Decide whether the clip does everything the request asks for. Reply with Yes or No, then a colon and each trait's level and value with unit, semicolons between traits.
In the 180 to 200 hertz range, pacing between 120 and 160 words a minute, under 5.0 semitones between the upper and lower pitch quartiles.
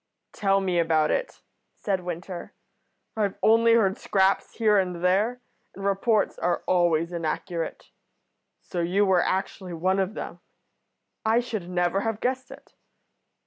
Yes: high, 190 Hz; average, 140 wpm; average, 3.5 semitones